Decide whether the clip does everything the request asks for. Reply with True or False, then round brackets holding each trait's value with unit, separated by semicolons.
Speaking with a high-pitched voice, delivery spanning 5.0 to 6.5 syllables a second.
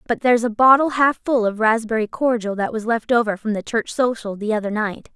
True (225 Hz; 5.7 syllables/s)